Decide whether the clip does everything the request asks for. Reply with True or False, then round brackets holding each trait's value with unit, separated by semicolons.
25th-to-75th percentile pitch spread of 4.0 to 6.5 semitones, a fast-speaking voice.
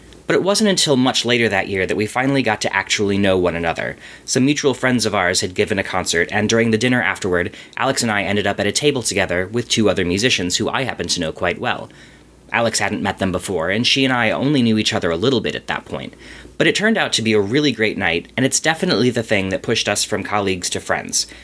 True (4.5 semitones; 255 wpm)